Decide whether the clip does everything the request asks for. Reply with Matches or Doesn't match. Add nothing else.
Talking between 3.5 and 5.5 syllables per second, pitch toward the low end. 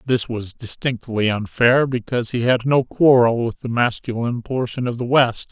Matches